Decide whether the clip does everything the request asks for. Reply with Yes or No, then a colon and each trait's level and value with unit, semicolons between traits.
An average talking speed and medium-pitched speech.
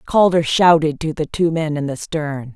No: fast, 210 wpm; medium, 155 Hz